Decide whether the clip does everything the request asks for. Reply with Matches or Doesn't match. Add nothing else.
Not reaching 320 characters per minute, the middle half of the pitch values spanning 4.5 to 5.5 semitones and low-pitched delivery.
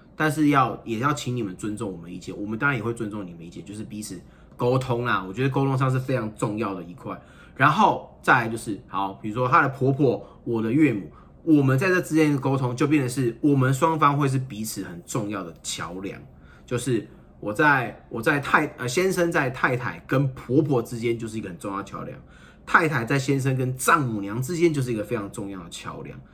Doesn't match